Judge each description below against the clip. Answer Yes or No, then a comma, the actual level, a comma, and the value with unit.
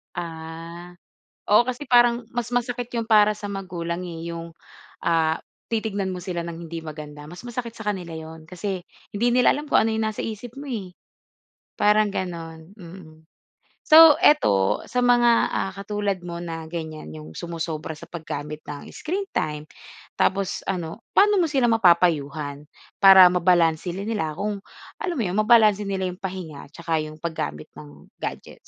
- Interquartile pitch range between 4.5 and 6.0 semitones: Yes, average, 5.1 semitones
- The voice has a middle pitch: Yes, medium, 180 Hz